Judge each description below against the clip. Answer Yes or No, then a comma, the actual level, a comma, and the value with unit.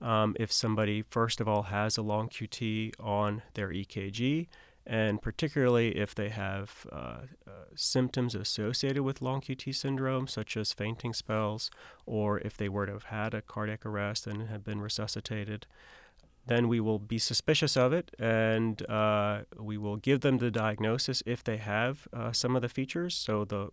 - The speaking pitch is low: Yes, low, 110 Hz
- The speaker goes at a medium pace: Yes, average, 175 wpm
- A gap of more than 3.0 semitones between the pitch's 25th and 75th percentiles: No, average, 2.7 semitones